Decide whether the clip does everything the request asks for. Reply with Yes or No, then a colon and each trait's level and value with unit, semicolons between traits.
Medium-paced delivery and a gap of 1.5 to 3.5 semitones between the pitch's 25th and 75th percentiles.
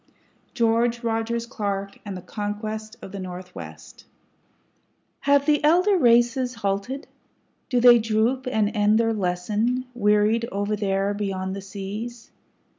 No: slow, 125 wpm; average, 3.2 semitones